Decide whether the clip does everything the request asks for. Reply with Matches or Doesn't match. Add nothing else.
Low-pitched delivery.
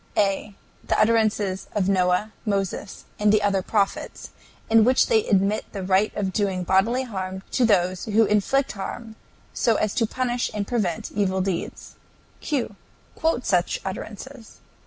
Doesn't match